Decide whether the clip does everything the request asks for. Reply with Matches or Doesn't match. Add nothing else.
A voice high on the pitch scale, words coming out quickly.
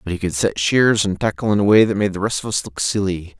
Doesn't match